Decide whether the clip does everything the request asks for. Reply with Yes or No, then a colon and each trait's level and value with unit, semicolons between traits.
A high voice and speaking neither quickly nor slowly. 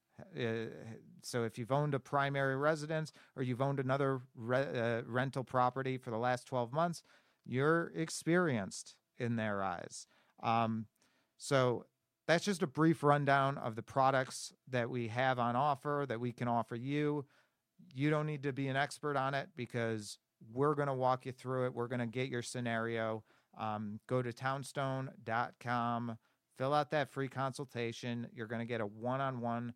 No: low, 130 Hz; average, 170 wpm